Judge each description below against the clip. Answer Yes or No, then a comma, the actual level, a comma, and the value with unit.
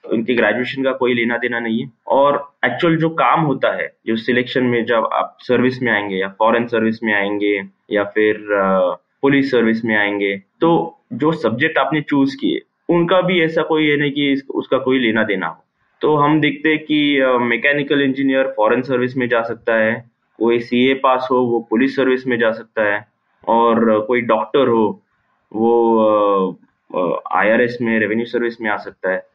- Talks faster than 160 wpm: Yes, fast, 190 wpm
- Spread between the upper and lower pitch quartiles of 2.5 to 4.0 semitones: Yes, average, 3.4 semitones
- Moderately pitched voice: No, low, 120 Hz